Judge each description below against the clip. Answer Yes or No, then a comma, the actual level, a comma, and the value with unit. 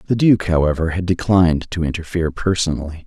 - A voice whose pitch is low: Yes, very low, 85 Hz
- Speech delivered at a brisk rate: No, average, 155 wpm